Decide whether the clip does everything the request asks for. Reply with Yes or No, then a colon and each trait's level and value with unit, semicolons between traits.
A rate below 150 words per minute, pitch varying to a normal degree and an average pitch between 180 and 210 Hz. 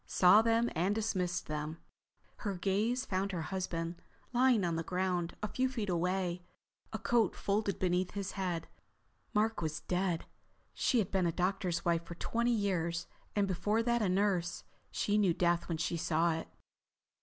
No: average, 165 wpm; average, 3.3 semitones; medium, 185 Hz